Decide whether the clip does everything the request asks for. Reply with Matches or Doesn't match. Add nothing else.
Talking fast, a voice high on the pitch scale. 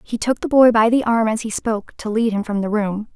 Matches